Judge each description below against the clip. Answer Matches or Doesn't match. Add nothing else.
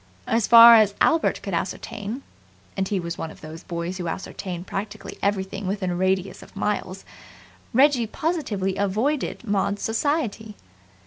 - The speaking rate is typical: Matches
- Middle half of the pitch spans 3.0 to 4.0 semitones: Matches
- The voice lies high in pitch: Matches